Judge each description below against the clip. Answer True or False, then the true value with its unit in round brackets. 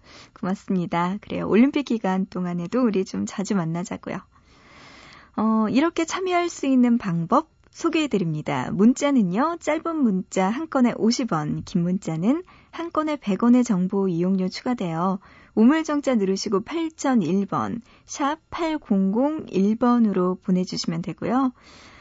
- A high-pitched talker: True (220 Hz)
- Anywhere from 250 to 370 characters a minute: True (265 characters per minute)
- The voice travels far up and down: True (6.8 semitones)